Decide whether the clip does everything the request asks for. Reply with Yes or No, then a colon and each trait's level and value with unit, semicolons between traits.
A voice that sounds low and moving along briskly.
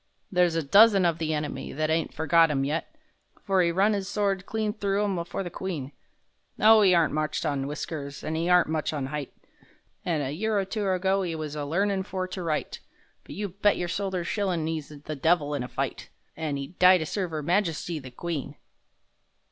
No: medium, 170 Hz; fast, 210 wpm